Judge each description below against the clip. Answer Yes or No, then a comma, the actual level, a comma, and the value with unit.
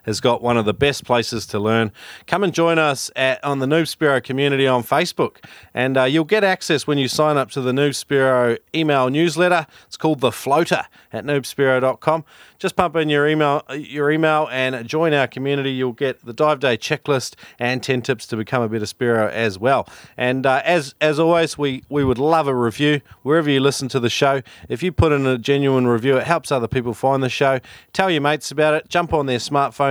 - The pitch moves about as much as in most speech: Yes, average, 3.2 semitones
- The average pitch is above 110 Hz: Yes, medium, 140 Hz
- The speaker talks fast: Yes, fast, 220 wpm